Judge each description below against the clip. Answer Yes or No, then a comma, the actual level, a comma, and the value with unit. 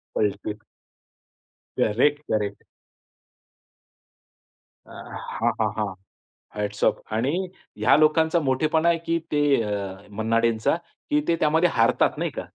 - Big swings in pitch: Yes, wide, 6.6 semitones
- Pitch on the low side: Yes, low, 115 Hz